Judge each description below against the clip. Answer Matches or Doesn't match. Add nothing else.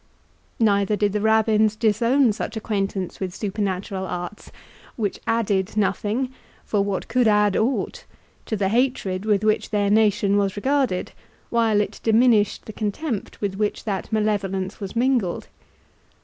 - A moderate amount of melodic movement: Doesn't match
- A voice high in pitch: Matches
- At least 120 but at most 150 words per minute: Matches